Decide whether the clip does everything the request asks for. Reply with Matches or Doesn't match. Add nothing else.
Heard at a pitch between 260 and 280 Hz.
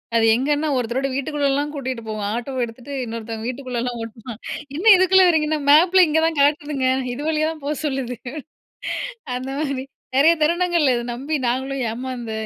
Matches